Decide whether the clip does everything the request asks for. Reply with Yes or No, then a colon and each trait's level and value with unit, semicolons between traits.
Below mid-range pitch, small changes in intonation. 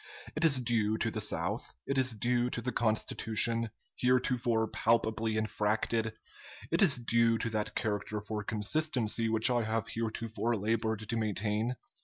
Yes: low, 115 Hz; narrow, 1.7 semitones